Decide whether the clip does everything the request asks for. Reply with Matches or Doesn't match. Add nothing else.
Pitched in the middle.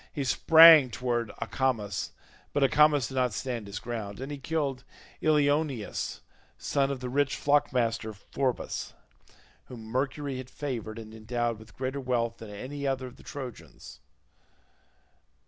Doesn't match